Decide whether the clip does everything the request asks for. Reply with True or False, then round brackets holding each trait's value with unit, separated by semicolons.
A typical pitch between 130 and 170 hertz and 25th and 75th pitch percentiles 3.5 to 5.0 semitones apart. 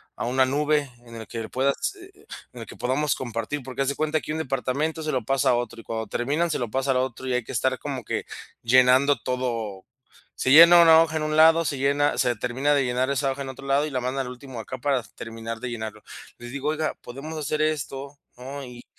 False (135 Hz; 3.0 semitones)